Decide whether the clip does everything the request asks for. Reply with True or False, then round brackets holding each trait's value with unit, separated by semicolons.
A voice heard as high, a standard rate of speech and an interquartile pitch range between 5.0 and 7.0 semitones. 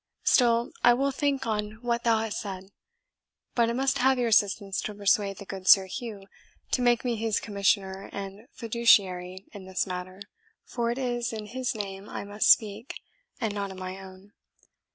False (210 Hz; 180 wpm; 3.5 semitones)